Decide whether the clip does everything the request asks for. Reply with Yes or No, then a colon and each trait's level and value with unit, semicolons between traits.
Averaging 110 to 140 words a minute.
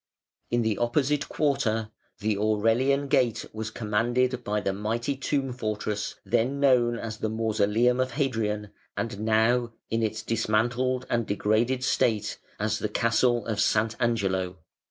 Yes: slow, 135 wpm